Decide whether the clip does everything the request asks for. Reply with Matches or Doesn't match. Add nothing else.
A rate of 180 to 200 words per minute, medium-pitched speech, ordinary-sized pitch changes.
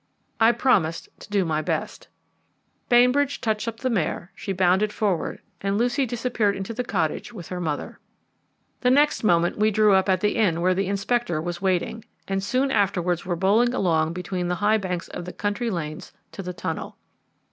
Doesn't match